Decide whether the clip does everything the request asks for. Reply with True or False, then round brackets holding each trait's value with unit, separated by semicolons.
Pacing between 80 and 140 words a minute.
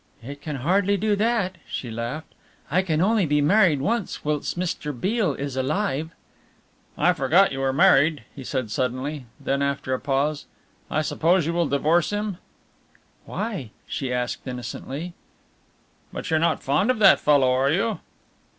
False (160 wpm)